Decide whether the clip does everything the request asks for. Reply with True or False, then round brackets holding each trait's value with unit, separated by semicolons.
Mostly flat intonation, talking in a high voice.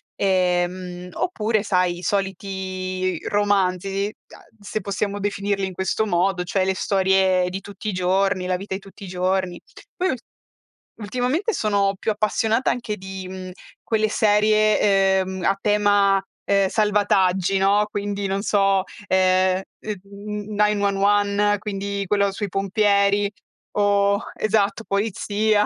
True (1.7 semitones; 200 Hz)